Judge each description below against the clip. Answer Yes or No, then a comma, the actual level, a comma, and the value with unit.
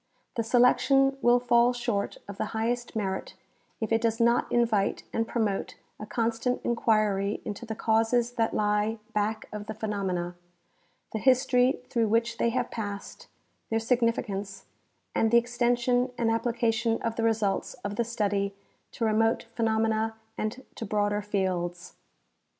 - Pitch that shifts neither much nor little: No, narrow, 2.3 semitones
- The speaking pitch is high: Yes, high, 225 Hz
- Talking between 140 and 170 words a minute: Yes, average, 145 wpm